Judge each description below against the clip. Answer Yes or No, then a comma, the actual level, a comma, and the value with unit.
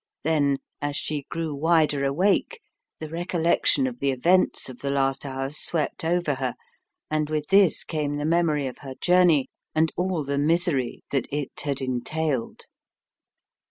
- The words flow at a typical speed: Yes, average, 155 wpm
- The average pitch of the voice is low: No, medium, 150 Hz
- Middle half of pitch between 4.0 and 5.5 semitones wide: No, average, 3.2 semitones